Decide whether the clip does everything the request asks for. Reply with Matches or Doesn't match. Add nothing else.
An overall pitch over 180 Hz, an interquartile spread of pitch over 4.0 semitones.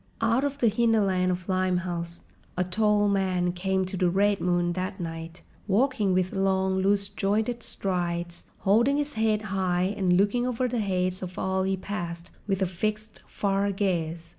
Doesn't match